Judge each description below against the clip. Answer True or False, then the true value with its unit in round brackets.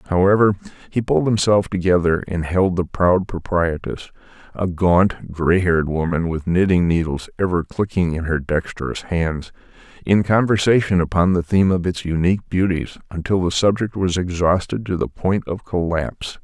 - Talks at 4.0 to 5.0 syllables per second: True (4.9 syllables/s)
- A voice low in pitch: True (90 Hz)